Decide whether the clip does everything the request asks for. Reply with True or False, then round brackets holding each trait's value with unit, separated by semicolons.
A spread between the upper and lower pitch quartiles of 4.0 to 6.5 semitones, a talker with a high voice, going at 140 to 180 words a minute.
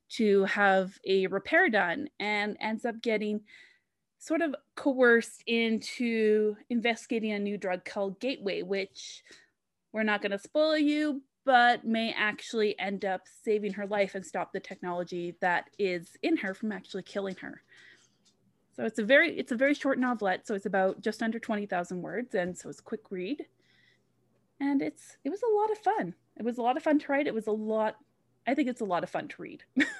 False (4.5 semitones; 215 Hz; 190 wpm)